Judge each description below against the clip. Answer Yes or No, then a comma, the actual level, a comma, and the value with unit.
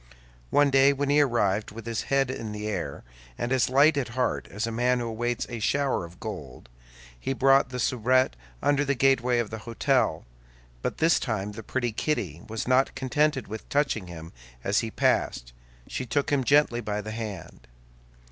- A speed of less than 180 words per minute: No, average, 185 wpm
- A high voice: No, low, 120 Hz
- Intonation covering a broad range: No, average, 4.0 semitones